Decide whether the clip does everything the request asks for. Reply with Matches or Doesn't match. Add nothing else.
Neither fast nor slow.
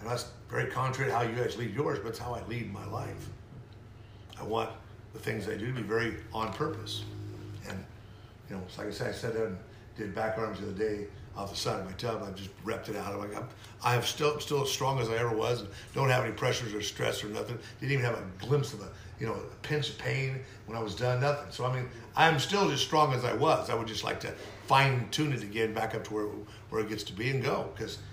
Doesn't match